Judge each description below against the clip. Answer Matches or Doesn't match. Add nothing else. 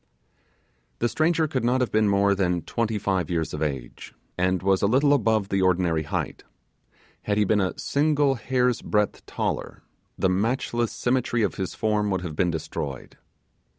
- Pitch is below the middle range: Matches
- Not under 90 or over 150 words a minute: Doesn't match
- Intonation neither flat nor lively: Matches